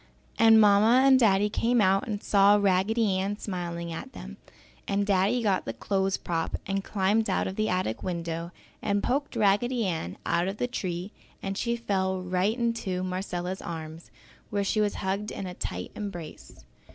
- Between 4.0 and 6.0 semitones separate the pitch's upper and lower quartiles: No, average, 2.9 semitones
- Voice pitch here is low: No, high, 195 Hz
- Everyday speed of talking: Yes, average, 170 wpm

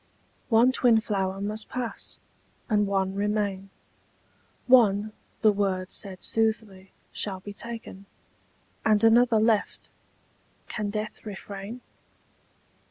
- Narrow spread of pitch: Yes, narrow, 2.3 semitones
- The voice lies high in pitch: Yes, high, 210 Hz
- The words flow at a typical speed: No, slow, 100 wpm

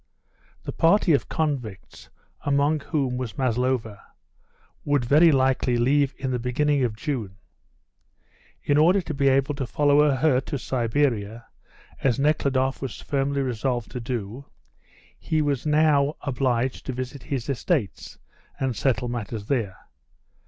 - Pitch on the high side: No, low, 135 Hz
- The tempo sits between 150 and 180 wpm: No, slow, 135 wpm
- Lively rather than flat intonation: No, average, 2.9 semitones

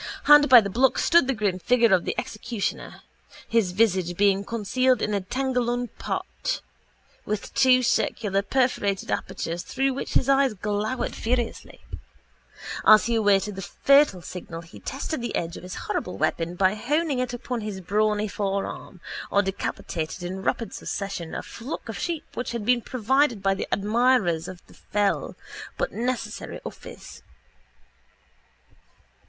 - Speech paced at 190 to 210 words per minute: No, average, 150 wpm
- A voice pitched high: Yes, high, 215 Hz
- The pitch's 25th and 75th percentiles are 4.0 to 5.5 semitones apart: Yes, average, 4.5 semitones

